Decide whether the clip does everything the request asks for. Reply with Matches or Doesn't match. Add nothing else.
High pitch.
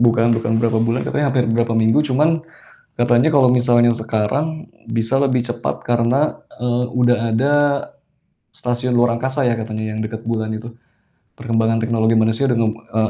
Doesn't match